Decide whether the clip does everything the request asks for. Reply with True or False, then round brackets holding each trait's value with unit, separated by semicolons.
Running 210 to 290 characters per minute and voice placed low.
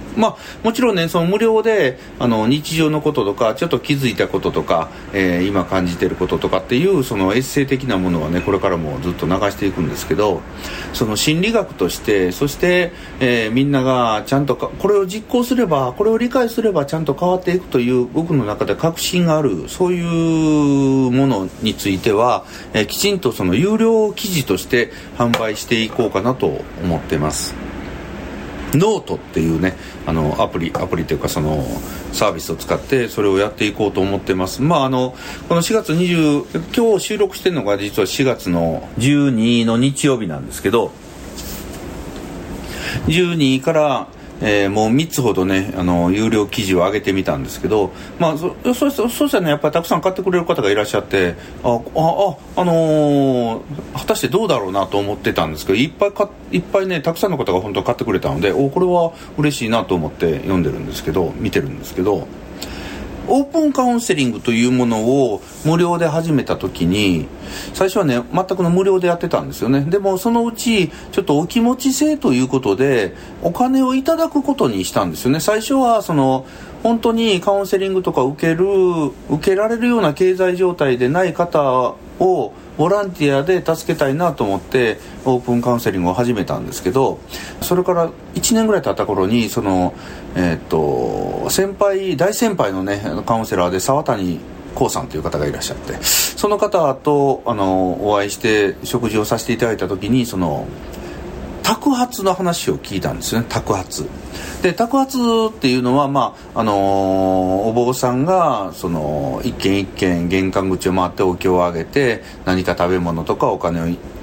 False (360 characters per minute; 130 Hz)